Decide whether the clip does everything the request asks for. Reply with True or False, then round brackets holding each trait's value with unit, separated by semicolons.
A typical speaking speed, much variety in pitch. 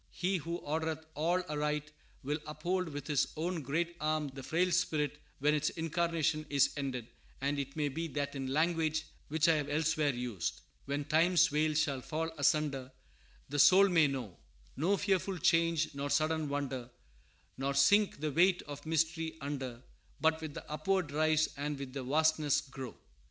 False (165 wpm; 2.5 semitones)